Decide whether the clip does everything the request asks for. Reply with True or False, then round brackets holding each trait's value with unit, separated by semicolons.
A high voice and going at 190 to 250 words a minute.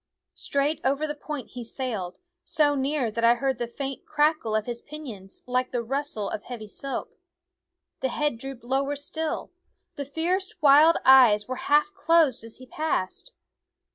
False (270 Hz; 165 wpm)